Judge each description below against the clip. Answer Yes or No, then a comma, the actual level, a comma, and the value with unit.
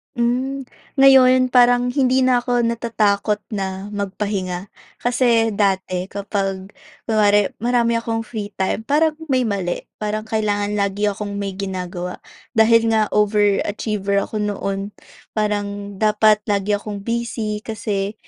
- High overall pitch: Yes, high, 210 Hz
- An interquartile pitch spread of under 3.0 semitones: Yes, narrow, 2.6 semitones